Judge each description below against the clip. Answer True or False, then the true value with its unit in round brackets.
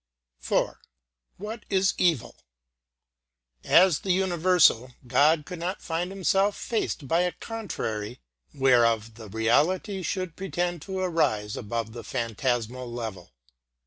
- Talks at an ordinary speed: False (115 wpm)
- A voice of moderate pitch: True (160 Hz)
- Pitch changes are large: True (8.2 semitones)